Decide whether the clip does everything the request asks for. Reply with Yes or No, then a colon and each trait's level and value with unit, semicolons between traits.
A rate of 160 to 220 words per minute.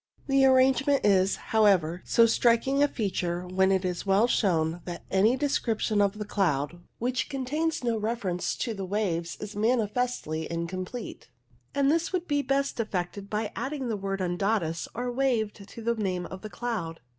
Yes: average, 170 wpm